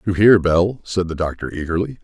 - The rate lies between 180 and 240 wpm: Yes, fast, 205 wpm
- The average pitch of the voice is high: No, very low, 95 Hz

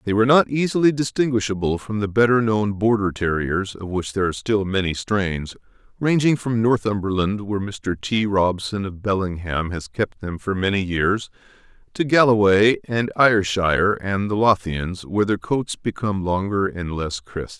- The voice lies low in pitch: Yes, low, 105 Hz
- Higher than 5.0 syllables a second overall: No, 4.8 syllables/s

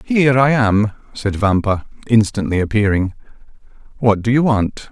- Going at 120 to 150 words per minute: Yes, slow, 135 wpm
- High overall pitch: No, low, 110 Hz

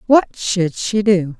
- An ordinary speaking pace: Yes, average, 170 wpm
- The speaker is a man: No, female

